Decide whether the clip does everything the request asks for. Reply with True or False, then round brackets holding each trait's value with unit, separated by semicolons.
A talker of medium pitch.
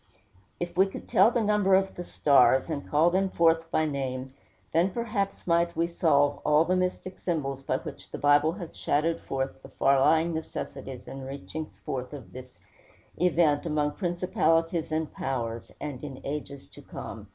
True (155 Hz)